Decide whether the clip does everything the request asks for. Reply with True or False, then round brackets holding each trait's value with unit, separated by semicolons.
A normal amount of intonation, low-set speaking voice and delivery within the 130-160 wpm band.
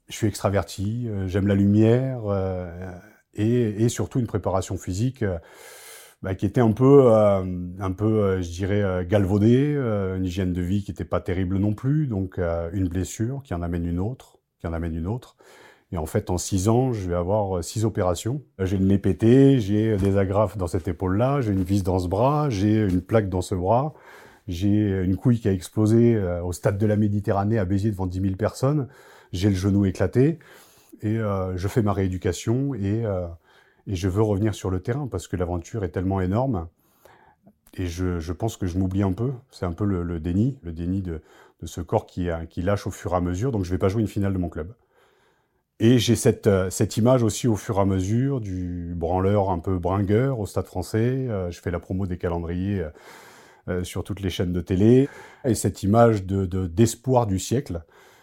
False (3.3 semitones; 100 Hz; 220 wpm)